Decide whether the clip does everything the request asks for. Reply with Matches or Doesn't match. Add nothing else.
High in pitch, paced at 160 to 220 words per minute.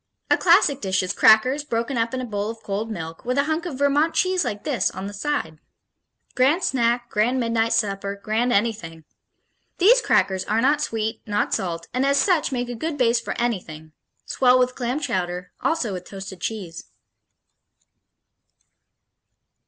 Matches